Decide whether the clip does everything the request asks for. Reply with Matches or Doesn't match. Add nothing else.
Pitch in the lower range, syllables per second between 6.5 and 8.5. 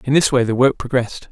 Matches